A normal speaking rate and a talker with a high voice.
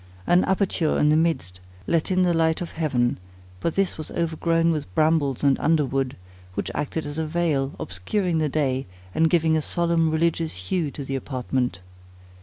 No: average, 175 wpm; medium, 155 Hz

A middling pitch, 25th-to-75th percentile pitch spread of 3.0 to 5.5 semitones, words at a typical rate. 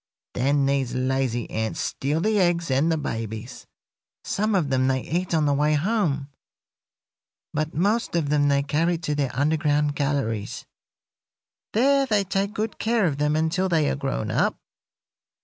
Yes: medium, 150 Hz; average, 4.3 semitones; average, 160 wpm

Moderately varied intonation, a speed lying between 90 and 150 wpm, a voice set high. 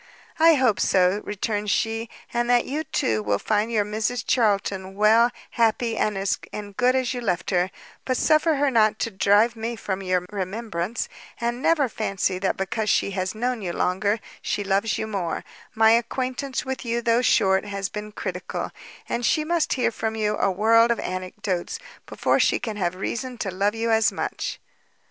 No: average, 3.3 semitones; average, 180 wpm; high, 215 Hz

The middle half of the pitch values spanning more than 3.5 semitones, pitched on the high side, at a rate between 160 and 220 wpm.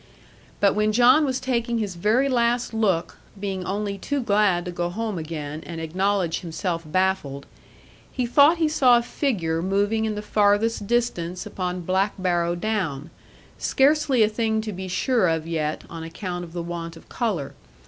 Yes: average, 4.9 semitones; high, 195 Hz; average, 170 wpm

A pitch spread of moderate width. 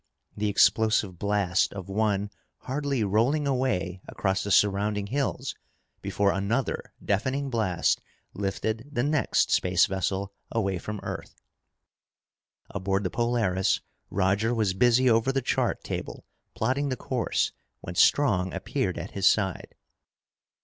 Yes: average, 4.0 semitones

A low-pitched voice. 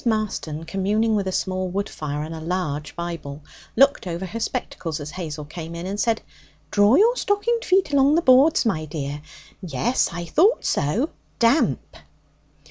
No: high, 190 Hz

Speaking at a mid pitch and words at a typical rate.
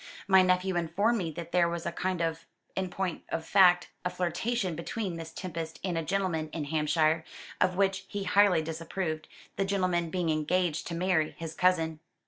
Yes: medium, 175 Hz; average, 180 wpm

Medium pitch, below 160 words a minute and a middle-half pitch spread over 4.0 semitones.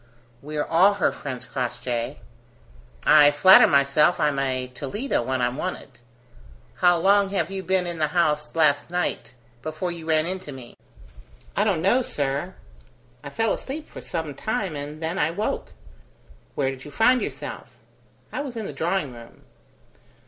No: medium, 155 Hz; average, 165 wpm; average, 5.2 semitones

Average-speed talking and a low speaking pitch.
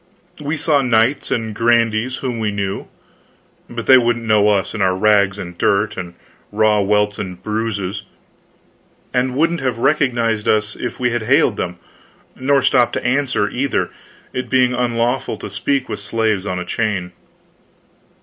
Yes: average, 160 wpm; low, 115 Hz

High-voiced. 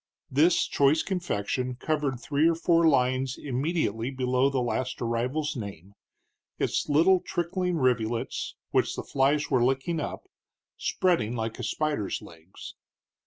No: low, 135 Hz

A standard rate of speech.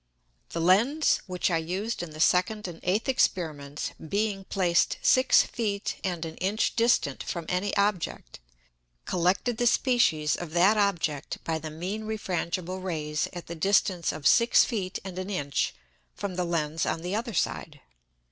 Yes: average, 160 wpm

